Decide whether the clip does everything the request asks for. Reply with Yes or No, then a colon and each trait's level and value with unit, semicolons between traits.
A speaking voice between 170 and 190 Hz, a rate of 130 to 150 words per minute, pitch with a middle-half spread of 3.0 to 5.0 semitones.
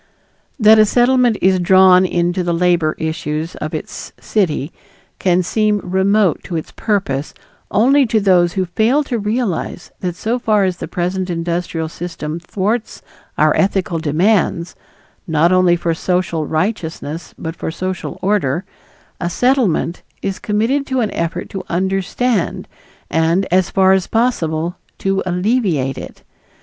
Yes: medium, 185 Hz; average, 140 wpm; average, 3.8 semitones